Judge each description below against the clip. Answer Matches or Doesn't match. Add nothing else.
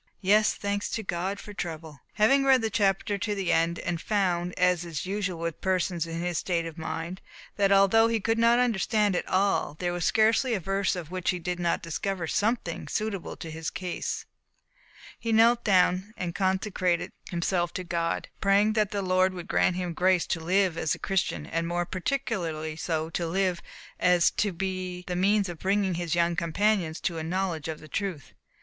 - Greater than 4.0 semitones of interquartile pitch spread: Doesn't match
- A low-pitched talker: Doesn't match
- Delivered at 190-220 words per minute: Matches